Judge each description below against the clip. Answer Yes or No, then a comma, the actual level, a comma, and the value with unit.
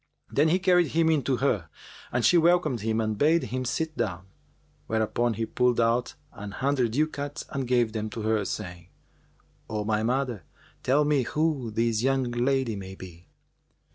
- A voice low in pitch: Yes, low, 120 Hz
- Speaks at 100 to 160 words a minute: No, average, 170 wpm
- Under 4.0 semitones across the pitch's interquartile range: No, average, 4.6 semitones